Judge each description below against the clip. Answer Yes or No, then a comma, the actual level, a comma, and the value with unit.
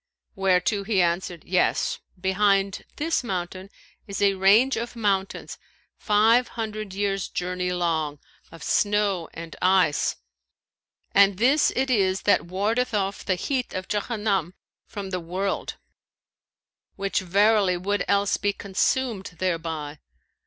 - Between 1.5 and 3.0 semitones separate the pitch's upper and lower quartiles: Yes, narrow, 2.4 semitones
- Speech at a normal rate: No, slow, 125 wpm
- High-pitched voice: Yes, high, 195 Hz